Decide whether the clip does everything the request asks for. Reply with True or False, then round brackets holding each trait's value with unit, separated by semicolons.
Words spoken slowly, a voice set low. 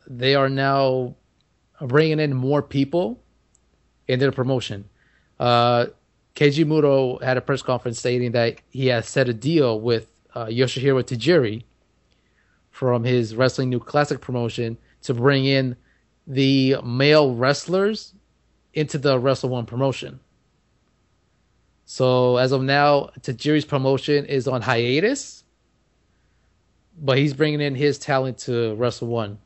True (130 wpm; 130 Hz)